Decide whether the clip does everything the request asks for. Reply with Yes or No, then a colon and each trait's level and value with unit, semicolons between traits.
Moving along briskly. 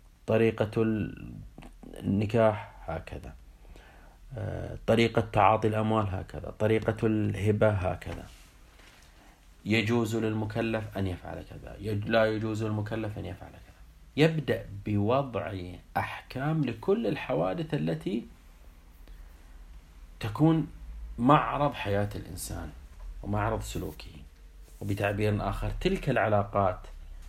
No: average, 80 wpm